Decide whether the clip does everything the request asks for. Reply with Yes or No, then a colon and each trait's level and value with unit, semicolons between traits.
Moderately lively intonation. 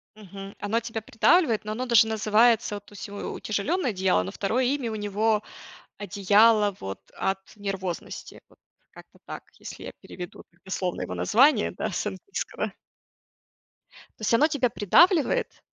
Yes: average, 3.1 semitones